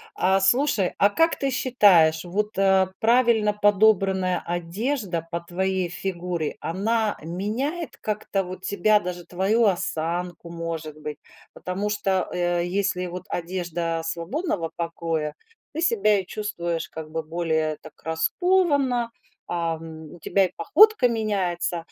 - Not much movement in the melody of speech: No, average, 4.0 semitones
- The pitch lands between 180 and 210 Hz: Yes, medium, 185 Hz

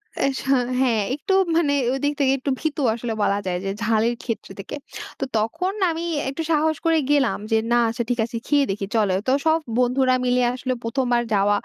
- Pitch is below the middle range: No, very high, 255 Hz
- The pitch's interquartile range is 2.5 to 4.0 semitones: No, average, 4.4 semitones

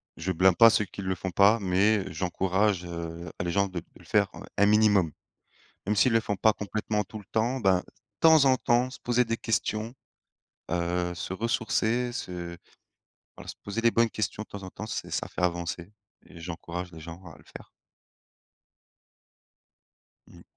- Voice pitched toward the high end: No, low, 100 Hz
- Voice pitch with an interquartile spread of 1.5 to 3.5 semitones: No, average, 4.1 semitones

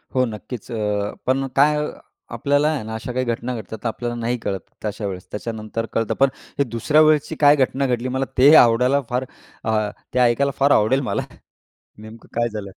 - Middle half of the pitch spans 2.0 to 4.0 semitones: Yes, average, 3.6 semitones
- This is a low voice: Yes, low, 120 Hz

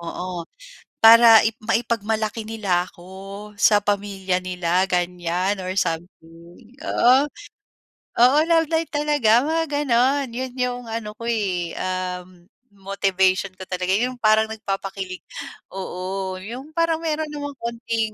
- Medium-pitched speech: No, high, 210 Hz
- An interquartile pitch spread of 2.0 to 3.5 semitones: No, average, 4.7 semitones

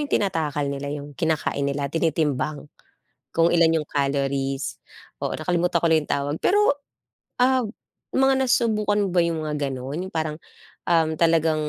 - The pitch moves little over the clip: No, average, 3.3 semitones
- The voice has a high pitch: No, medium, 160 Hz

